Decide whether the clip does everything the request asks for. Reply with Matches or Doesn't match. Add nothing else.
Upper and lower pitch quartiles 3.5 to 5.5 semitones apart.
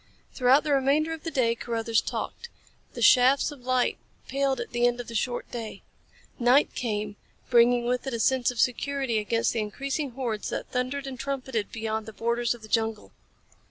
Doesn't match